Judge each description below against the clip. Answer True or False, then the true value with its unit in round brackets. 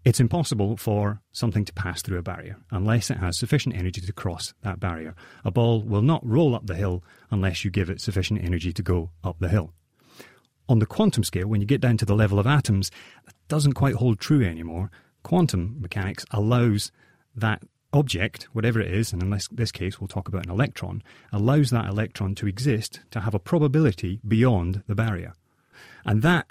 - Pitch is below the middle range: True (105 Hz)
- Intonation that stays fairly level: False (3.9 semitones)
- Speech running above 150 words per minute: True (195 wpm)